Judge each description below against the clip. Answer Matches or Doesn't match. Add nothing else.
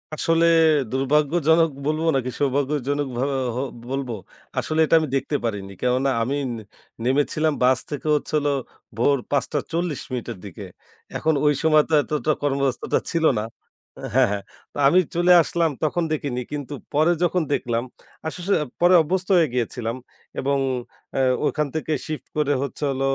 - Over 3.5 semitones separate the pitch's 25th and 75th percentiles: Doesn't match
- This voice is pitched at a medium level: Matches